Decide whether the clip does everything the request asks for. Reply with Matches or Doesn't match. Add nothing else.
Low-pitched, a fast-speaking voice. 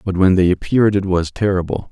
Matches